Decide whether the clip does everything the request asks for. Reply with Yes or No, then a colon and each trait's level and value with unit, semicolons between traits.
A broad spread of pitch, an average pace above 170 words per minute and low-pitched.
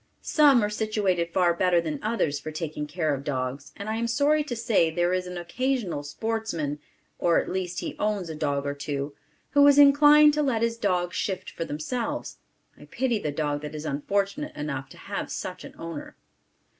No: wide, 7.2 semitones; average, 195 wpm; medium, 180 Hz